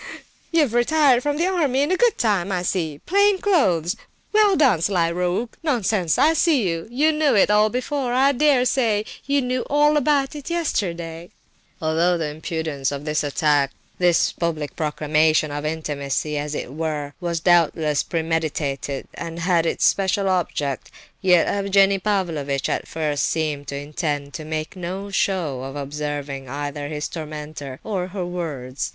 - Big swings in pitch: Yes, wide, 8.1 semitones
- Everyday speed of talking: Yes, average, 155 wpm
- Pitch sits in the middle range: Yes, medium, 170 Hz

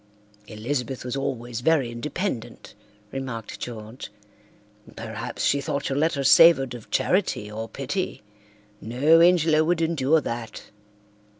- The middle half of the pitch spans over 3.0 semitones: Yes, average, 5.3 semitones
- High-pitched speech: No, low, 135 Hz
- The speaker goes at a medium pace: No, slow, 115 wpm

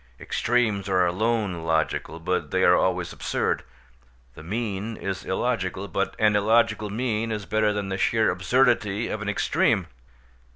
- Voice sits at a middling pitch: No, low, 105 Hz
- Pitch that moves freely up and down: No, average, 3.1 semitones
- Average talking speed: Yes, average, 150 wpm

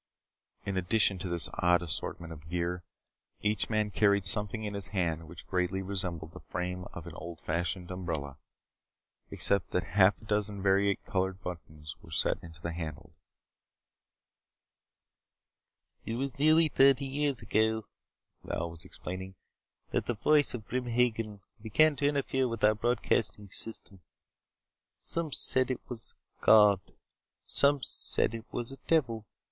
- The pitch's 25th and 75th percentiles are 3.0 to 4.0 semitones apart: No, average, 4.7 semitones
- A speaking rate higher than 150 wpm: No, average, 145 wpm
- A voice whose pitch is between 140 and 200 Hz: No, low, 100 Hz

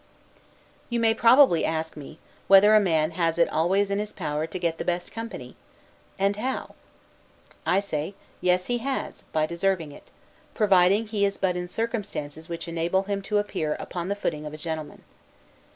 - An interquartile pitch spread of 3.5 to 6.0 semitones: Yes, average, 4.1 semitones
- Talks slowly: No, average, 175 wpm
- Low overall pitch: No, medium, 185 Hz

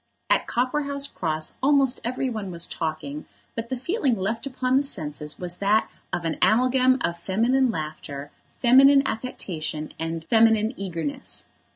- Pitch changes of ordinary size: No, wide, 7.9 semitones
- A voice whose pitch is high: Yes, high, 220 Hz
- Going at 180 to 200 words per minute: No, average, 145 wpm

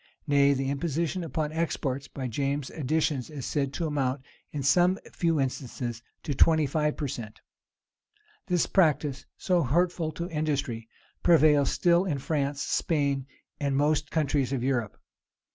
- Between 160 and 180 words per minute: No, average, 145 wpm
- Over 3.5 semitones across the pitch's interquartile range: No, average, 2.9 semitones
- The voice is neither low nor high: Yes, medium, 145 Hz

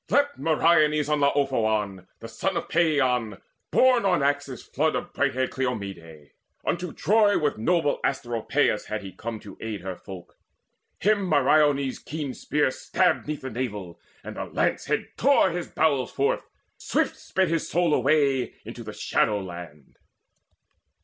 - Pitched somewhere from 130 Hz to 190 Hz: Yes, medium, 140 Hz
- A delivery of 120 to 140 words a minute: No, average, 150 wpm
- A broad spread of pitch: Yes, wide, 6.9 semitones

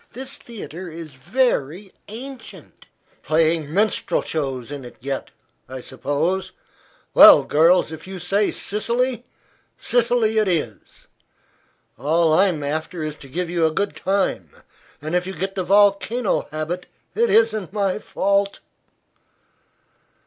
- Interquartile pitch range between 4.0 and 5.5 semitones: Yes, average, 4.9 semitones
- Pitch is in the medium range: Yes, medium, 180 Hz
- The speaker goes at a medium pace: No, slow, 125 wpm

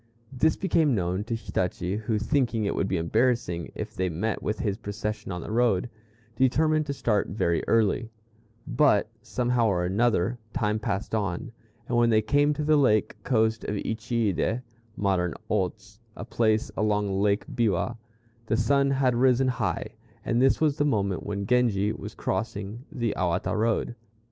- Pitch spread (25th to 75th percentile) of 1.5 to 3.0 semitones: No, average, 3.7 semitones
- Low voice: Yes, low, 110 Hz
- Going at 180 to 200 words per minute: No, average, 165 wpm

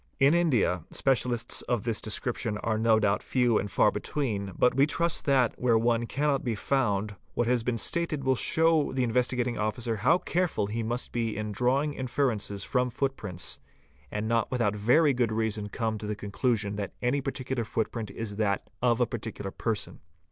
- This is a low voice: Yes, low, 115 Hz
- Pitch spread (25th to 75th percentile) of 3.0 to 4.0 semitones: Yes, average, 3.5 semitones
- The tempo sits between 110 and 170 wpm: No, average, 190 wpm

